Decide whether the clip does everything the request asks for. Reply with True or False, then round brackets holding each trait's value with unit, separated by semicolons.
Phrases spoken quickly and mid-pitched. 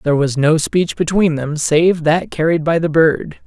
True (210 wpm; 160 Hz)